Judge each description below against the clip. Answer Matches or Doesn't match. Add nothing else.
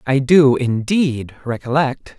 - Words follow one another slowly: Matches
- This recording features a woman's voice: Doesn't match